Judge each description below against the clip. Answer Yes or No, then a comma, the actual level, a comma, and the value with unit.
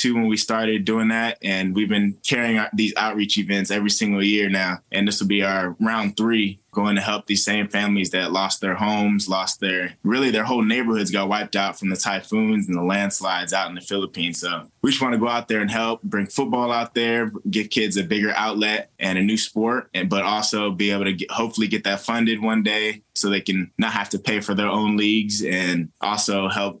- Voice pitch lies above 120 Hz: No, low, 105 Hz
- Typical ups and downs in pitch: No, narrow, 1.8 semitones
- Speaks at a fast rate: Yes, fast, 230 wpm